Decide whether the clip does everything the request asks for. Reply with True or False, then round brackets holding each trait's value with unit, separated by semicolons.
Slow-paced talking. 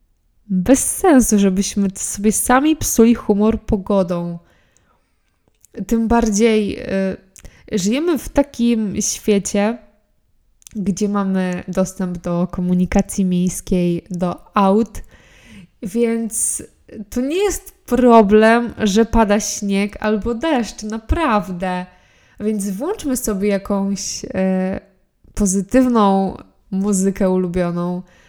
True (90 wpm)